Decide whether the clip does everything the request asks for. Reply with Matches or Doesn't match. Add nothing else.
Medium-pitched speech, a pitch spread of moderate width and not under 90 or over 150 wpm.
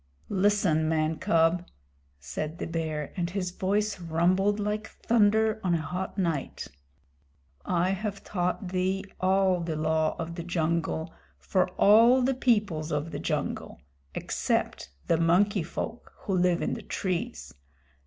Matches